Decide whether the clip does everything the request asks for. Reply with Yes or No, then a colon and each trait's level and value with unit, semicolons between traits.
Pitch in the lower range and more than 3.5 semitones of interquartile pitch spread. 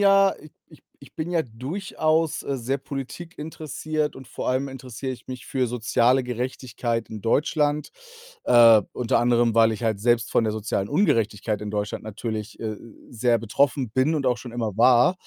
Yes: low, 125 Hz; average, 4.0 semitones